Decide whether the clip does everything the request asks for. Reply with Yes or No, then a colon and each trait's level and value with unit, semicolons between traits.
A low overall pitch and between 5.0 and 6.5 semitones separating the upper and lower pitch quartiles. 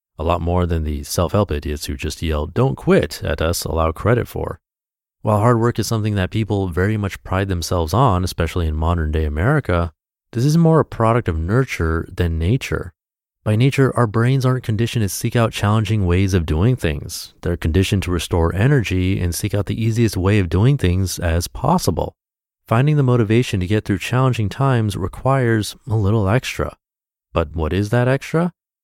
Yes: low, 100 Hz; wide, 5.4 semitones